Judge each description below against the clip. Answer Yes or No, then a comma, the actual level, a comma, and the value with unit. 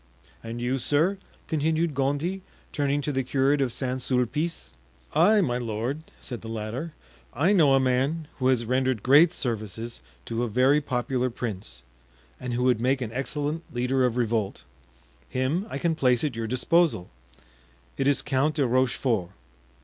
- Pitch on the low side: Yes, low, 130 Hz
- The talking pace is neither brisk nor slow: Yes, average, 160 wpm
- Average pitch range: Yes, average, 3.2 semitones